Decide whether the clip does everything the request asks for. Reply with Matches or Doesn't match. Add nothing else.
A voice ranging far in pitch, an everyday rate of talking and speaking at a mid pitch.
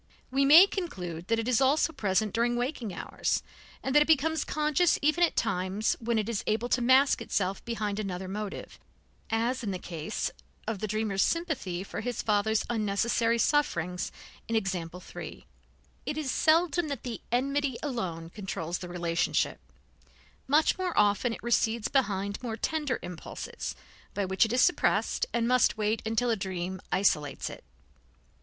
Doesn't match